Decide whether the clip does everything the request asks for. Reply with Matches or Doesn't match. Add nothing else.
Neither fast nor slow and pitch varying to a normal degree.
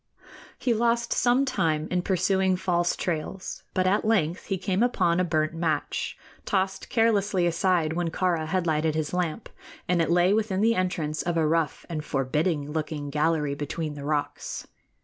Matches